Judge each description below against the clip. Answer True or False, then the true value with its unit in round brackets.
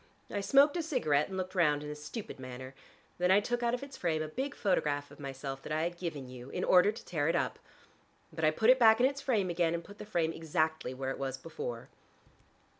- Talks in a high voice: False (165 Hz)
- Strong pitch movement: True (6.4 semitones)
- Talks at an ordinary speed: False (245 wpm)